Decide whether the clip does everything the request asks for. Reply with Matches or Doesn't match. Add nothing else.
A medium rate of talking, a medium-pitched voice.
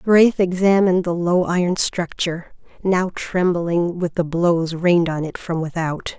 Matches